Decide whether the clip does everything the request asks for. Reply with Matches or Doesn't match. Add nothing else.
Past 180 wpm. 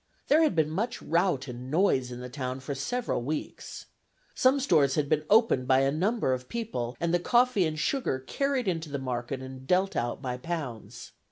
Matches